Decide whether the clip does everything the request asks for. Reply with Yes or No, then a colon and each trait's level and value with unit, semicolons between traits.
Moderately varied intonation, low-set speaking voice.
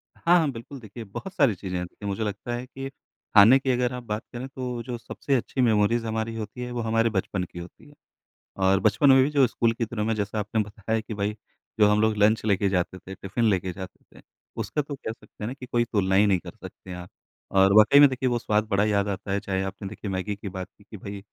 Yes: average, 3.5 semitones; low, 110 Hz